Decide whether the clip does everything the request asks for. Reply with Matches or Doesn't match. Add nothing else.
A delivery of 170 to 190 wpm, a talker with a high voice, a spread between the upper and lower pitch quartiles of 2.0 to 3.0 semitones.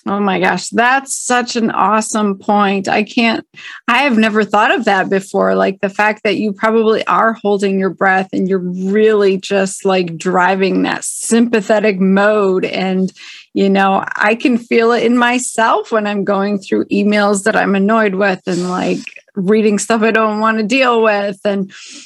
Matches